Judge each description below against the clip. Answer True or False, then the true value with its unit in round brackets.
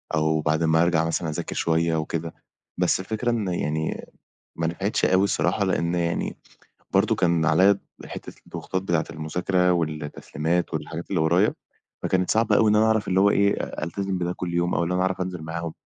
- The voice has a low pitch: True (85 Hz)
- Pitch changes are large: False (2.6 semitones)